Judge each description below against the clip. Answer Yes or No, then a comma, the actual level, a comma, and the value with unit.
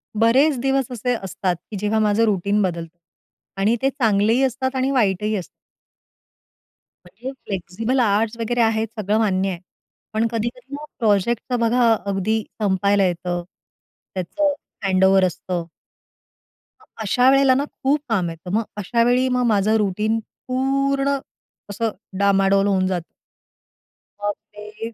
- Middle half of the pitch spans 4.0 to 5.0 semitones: Yes, average, 4.3 semitones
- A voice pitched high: Yes, high, 215 Hz